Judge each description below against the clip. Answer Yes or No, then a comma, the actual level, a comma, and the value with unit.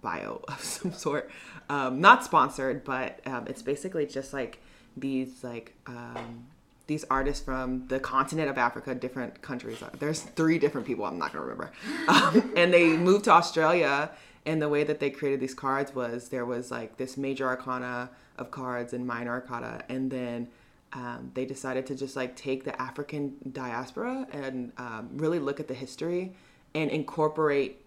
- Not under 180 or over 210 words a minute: No, average, 170 wpm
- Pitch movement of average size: Yes, average, 3.0 semitones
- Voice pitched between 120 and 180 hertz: Yes, low, 135 Hz